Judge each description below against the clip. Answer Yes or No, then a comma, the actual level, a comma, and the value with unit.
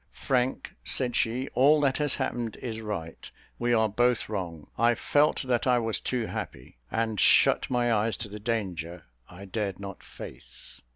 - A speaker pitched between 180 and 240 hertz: No, low, 115 Hz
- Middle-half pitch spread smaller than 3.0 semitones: No, average, 3.4 semitones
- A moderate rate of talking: Yes, average, 170 wpm